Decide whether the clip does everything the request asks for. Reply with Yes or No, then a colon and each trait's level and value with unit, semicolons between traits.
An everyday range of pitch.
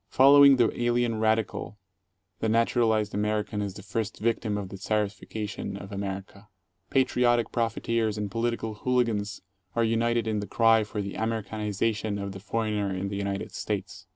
No: narrow, 2.1 semitones